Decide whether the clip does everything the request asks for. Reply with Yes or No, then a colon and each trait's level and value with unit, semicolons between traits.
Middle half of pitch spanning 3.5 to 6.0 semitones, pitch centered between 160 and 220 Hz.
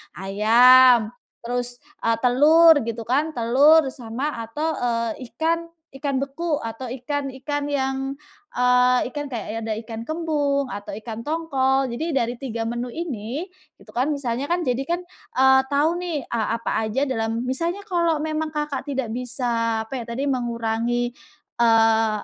No: average, 4.0 semitones; very high, 255 Hz